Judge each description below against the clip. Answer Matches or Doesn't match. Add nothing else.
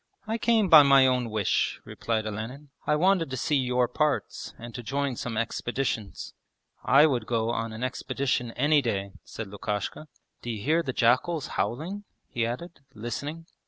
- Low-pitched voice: Matches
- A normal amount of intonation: Matches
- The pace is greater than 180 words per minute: Doesn't match